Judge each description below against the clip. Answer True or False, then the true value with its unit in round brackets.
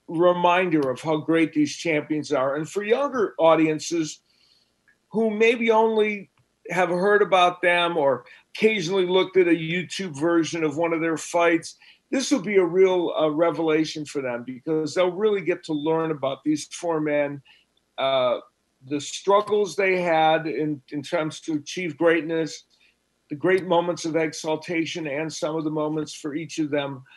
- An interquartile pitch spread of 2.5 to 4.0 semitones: True (3.1 semitones)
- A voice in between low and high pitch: True (165 Hz)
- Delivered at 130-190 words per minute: True (165 wpm)